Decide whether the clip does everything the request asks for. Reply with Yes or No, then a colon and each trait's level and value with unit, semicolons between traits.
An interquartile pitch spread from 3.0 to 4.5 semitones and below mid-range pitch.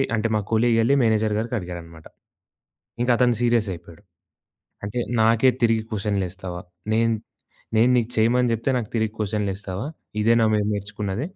No: narrow, 2.5 semitones; low, 110 Hz